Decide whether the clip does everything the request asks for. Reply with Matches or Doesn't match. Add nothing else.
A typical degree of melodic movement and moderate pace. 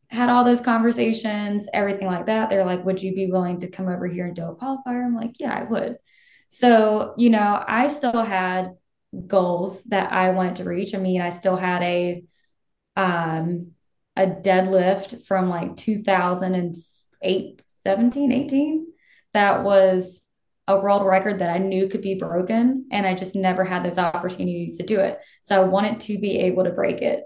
Matches